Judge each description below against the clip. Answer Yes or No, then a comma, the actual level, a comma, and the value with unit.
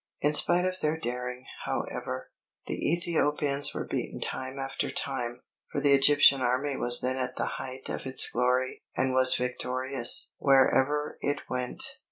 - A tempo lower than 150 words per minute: No, average, 155 wpm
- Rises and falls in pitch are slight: Yes, narrow, 2.3 semitones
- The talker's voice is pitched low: Yes, low, 130 Hz